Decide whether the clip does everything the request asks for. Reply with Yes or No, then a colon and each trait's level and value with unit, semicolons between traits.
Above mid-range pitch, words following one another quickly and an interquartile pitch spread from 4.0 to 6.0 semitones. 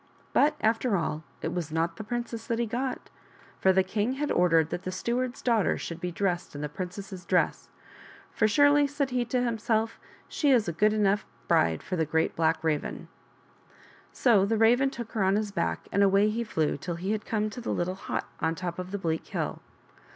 Yes: high, 200 Hz; fast, 215 wpm; average, 5.2 semitones